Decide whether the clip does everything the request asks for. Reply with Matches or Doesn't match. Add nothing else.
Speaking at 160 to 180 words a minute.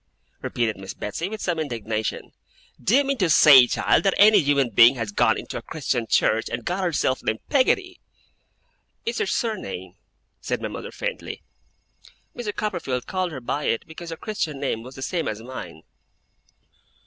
Matches